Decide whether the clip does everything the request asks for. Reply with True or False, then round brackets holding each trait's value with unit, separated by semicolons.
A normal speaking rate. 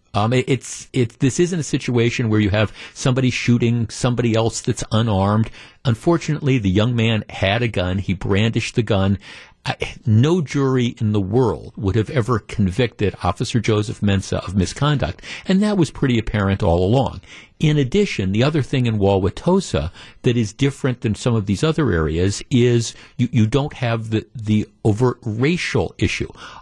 True (170 wpm)